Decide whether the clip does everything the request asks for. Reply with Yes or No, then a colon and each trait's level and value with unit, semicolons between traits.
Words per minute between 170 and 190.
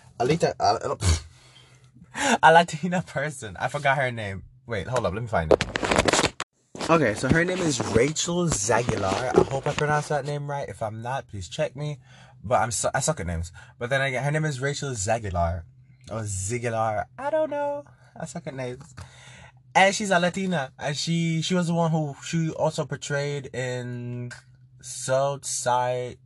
Yes: average, 175 wpm